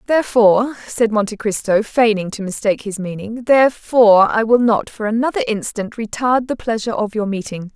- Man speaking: No, female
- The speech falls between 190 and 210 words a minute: No, average, 160 wpm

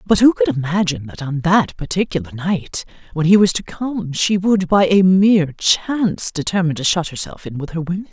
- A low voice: No, medium, 180 Hz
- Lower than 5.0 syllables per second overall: No, 5.4 syllables/s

